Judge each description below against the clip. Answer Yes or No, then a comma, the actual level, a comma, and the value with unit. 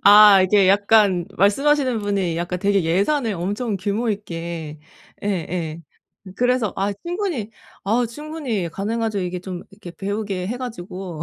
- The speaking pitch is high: Yes, high, 200 Hz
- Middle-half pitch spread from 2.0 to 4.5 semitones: Yes, average, 3.9 semitones